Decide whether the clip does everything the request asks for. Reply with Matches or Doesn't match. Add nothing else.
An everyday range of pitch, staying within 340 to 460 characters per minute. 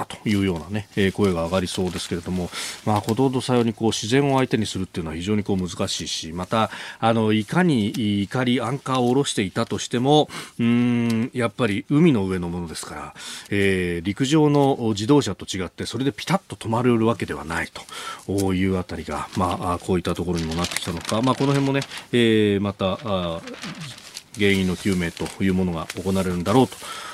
Matches